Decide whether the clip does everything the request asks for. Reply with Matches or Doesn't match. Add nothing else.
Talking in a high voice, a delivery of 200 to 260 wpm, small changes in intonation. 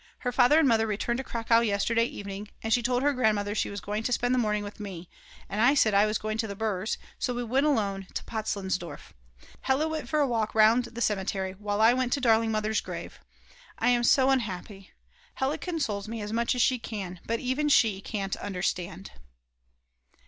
Doesn't match